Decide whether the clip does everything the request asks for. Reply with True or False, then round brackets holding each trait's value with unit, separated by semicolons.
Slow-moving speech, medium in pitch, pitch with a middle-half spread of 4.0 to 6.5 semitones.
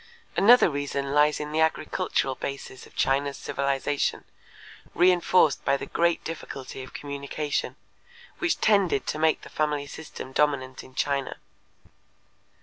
False (130 wpm; 145 Hz; 2.5 semitones)